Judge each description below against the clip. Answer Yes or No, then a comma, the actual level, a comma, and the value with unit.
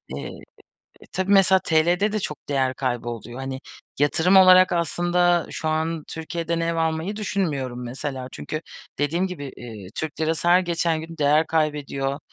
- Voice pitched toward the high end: No, medium, 160 Hz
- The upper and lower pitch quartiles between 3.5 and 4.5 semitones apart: Yes, average, 3.9 semitones